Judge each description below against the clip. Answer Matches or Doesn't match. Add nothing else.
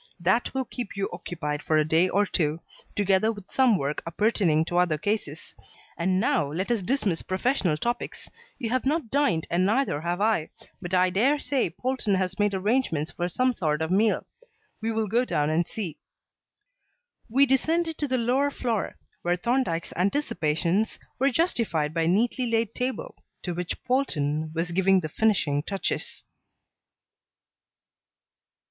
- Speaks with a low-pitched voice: Doesn't match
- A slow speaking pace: Doesn't match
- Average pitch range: Doesn't match